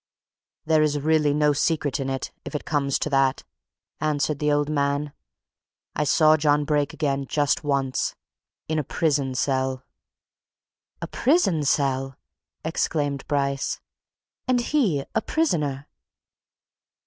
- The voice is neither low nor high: Yes, medium, 145 Hz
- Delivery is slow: Yes, slow, 125 wpm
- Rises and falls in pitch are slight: Yes, narrow, 1.9 semitones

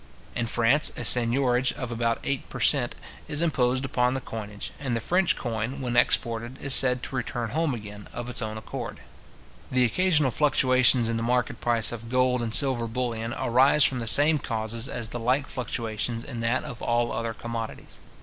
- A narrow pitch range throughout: Yes, narrow, 2.2 semitones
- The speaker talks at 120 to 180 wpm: No, average, 190 wpm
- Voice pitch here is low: Yes, low, 120 Hz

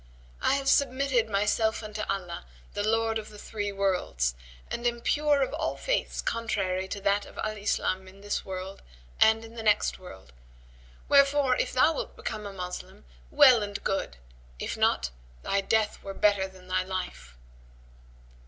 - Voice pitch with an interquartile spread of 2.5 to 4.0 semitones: Yes, average, 3.2 semitones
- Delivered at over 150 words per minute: Yes, average, 165 wpm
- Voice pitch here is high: Yes, high, 205 Hz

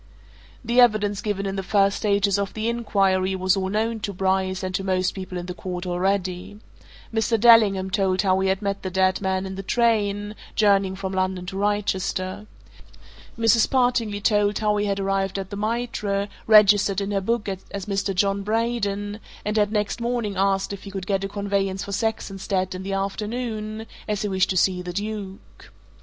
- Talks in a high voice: Yes, high, 200 Hz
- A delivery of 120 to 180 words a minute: No, average, 190 wpm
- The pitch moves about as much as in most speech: No, narrow, 1.7 semitones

